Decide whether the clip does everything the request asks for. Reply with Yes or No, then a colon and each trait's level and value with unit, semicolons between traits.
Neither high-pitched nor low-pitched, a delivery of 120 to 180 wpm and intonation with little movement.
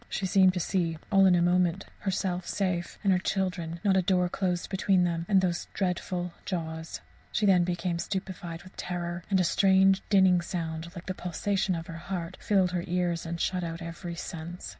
No: medium, 180 Hz; average, 195 wpm; narrow, 1.8 semitones